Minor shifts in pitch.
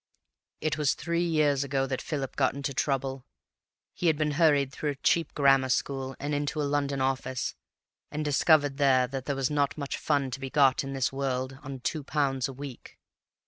Yes: narrow, 1.6 semitones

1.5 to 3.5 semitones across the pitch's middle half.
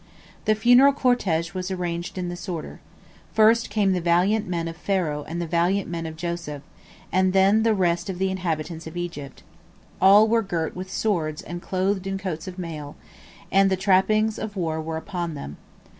Yes: average, 2.8 semitones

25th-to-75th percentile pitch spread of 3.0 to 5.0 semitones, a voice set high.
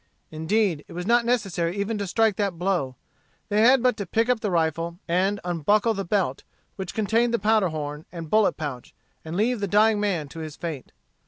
Yes: average, 4.7 semitones; high, 195 Hz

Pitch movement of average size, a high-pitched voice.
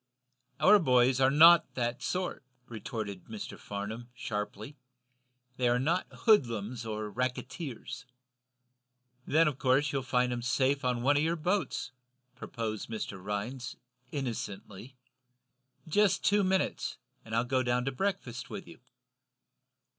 No: average, 4.1 semitones; low, 125 Hz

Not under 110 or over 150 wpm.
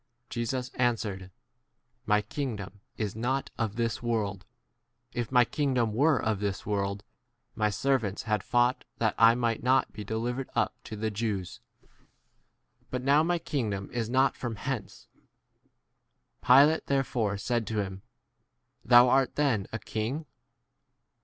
Yes: average, 140 wpm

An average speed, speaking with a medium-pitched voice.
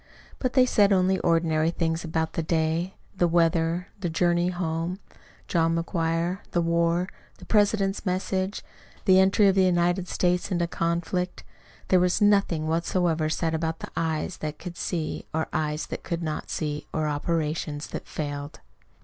Yes: average, 160 wpm; medium, 170 Hz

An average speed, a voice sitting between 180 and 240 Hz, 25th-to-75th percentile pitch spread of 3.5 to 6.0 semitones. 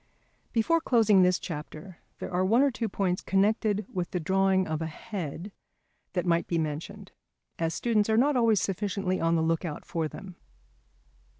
Yes: average, 185 wpm; high, 190 Hz; average, 4.1 semitones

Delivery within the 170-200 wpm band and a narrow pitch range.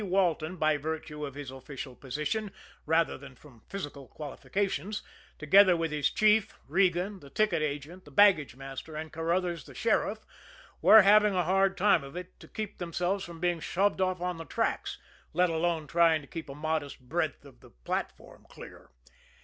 No: average, 175 wpm; average, 4.2 semitones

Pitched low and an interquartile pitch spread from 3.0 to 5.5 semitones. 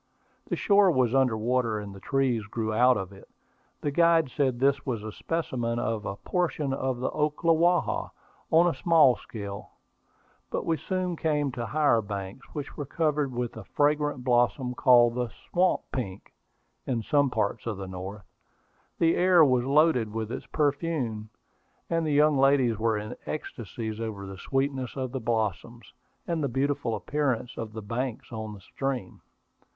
Yes: low, 125 Hz; average, 4.9 semitones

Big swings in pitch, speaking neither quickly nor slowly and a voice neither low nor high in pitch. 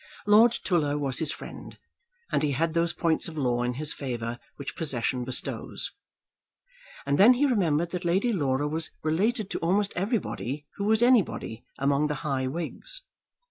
Yes: wide, 6.3 semitones; average, 165 wpm; medium, 160 Hz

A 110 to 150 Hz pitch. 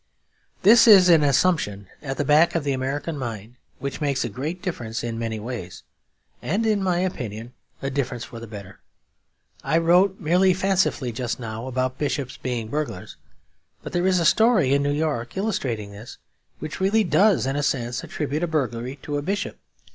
Yes: medium, 140 Hz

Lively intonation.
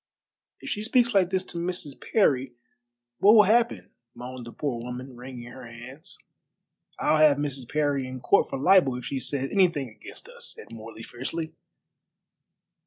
Yes: wide, 6.1 semitones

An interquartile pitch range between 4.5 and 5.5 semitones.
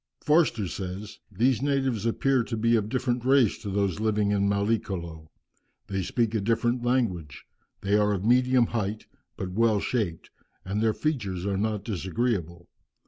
No: average, 3.6 semitones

